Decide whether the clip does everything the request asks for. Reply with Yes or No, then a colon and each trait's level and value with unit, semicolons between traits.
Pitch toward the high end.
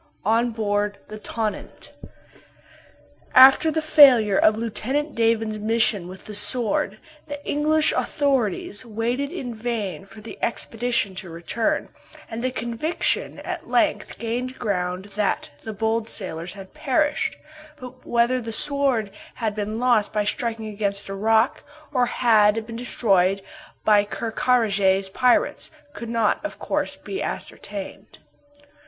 Yes: high, 225 Hz